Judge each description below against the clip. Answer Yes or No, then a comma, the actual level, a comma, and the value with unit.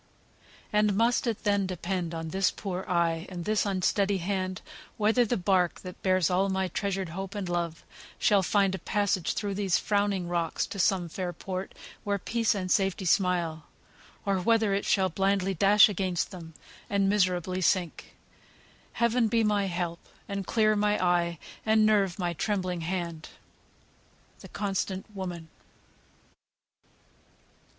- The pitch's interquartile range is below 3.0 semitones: Yes, narrow, 2.4 semitones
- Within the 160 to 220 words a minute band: No, average, 150 wpm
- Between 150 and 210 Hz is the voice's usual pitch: Yes, high, 190 Hz